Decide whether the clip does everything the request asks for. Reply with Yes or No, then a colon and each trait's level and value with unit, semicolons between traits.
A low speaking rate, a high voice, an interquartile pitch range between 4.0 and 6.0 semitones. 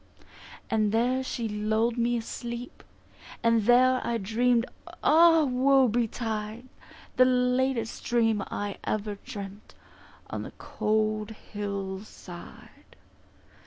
No: slow, 105 wpm; high, 230 Hz; average, 2.8 semitones